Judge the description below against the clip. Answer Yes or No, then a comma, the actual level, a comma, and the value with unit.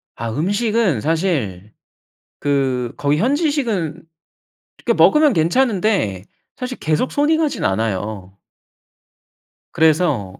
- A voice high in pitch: No, medium, 160 Hz